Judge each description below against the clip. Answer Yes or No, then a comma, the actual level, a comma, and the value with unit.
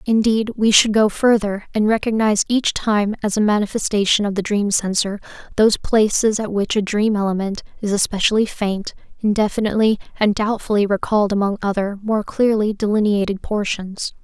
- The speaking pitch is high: Yes, high, 210 Hz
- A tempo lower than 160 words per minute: Yes, average, 150 wpm